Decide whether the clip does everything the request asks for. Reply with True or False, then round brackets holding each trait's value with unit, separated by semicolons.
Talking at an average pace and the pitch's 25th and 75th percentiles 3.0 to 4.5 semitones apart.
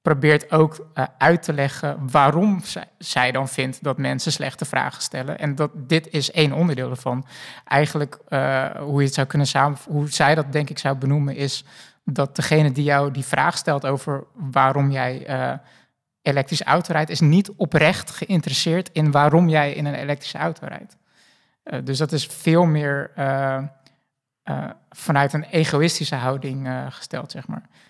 False (170 wpm; 2.4 semitones)